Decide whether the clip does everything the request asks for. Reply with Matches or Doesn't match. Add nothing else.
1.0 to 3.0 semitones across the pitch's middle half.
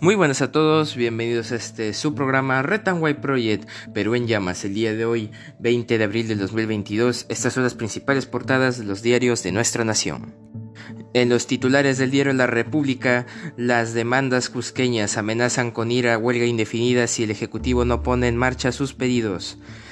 Matches